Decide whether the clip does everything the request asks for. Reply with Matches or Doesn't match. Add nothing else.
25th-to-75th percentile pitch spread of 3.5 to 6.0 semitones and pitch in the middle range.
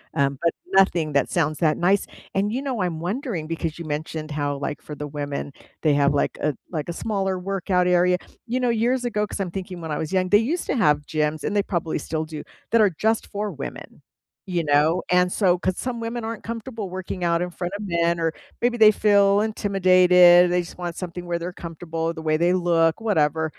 Matches